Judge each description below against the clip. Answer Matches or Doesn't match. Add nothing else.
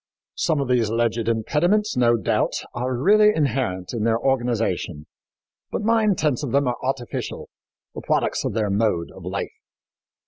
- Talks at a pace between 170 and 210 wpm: Doesn't match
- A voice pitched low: Matches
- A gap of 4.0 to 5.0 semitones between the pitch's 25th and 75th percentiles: Matches